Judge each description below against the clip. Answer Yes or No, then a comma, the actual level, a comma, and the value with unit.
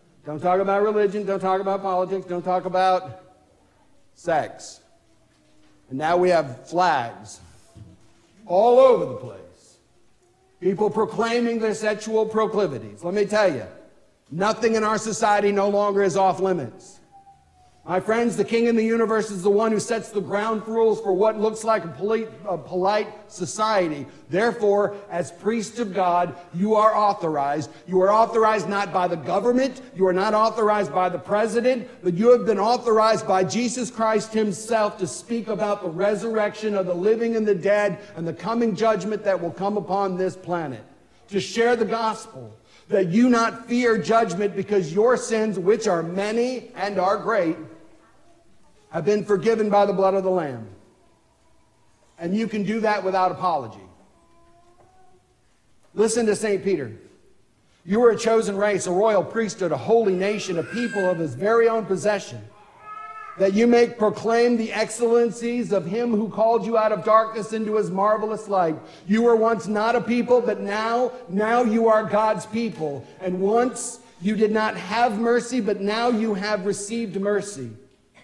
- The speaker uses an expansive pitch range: No, average, 3.1 semitones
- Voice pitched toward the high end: Yes, high, 210 Hz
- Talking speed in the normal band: Yes, average, 165 wpm